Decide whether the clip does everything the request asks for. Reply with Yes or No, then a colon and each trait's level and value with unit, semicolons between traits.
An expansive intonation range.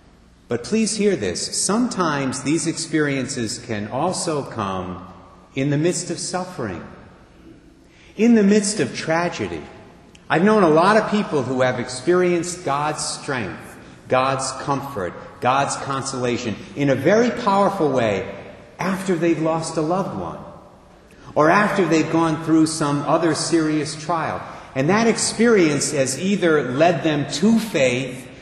Yes: wide, 5.7 semitones